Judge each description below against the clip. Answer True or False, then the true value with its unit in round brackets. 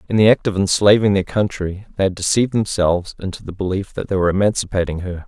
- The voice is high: False (95 Hz)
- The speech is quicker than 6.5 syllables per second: True (6.7 syllables/s)